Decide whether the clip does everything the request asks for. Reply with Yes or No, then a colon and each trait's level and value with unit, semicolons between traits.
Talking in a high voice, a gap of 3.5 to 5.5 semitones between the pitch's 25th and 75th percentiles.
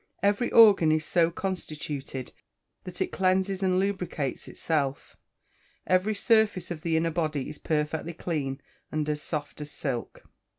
No: medium, 165 Hz; average, 3.8 semitones